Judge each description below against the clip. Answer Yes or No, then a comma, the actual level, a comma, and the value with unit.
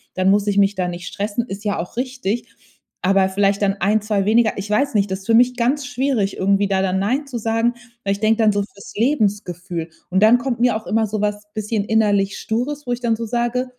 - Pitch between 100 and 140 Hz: No, high, 210 Hz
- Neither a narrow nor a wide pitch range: Yes, average, 3.2 semitones